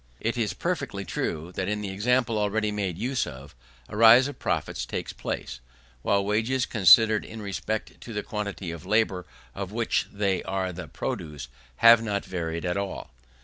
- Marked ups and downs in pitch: No, average, 3.2 semitones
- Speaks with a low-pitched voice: Yes, low, 105 Hz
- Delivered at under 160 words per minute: No, average, 175 wpm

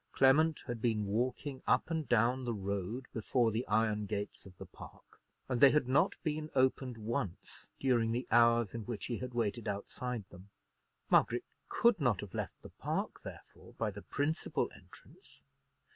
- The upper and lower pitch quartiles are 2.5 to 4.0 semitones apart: Yes, average, 3.7 semitones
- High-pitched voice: No, low, 120 Hz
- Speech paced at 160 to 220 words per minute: Yes, average, 170 wpm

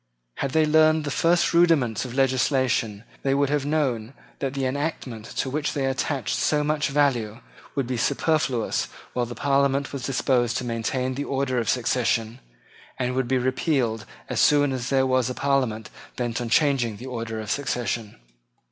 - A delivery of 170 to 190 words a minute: Yes, average, 175 wpm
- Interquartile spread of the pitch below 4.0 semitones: Yes, average, 2.8 semitones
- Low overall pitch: Yes, low, 130 Hz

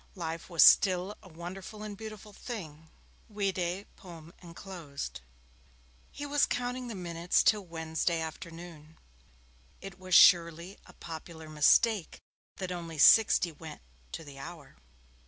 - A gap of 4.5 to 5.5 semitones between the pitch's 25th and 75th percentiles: No, average, 3.3 semitones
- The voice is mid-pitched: Yes, medium, 175 Hz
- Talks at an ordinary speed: No, slow, 125 wpm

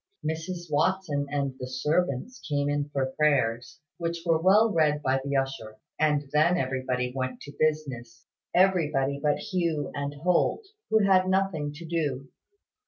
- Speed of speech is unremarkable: Yes, average, 150 wpm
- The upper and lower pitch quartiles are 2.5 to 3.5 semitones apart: No, average, 4.0 semitones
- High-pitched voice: No, medium, 150 Hz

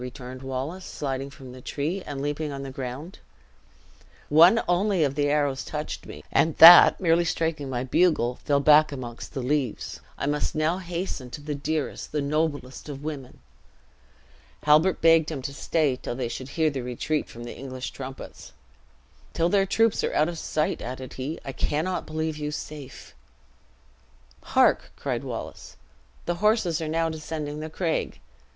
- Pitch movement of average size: Yes, average, 3.3 semitones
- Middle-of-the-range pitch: Yes, medium, 150 Hz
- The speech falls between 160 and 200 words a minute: Yes, average, 165 wpm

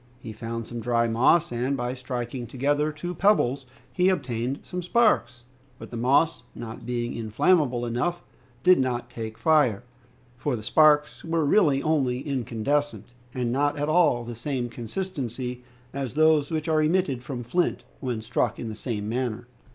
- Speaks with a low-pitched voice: Yes, low, 130 Hz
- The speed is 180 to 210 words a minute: No, average, 165 wpm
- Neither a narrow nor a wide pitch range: Yes, average, 4.3 semitones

